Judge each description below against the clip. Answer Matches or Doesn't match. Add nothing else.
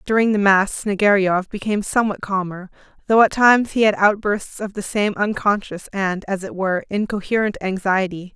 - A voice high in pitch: Matches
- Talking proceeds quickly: Doesn't match